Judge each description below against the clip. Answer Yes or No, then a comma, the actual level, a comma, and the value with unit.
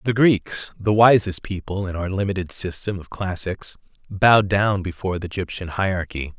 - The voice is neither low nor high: No, very low, 95 Hz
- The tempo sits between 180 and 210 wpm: No, average, 160 wpm